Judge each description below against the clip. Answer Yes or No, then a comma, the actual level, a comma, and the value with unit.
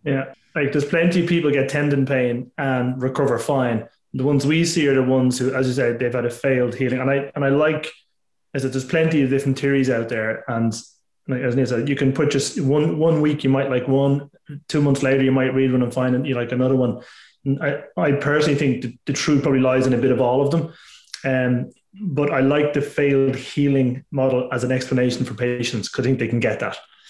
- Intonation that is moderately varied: No, narrow, 2.2 semitones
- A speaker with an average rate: No, fast, 245 wpm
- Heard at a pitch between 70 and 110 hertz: No, low, 135 Hz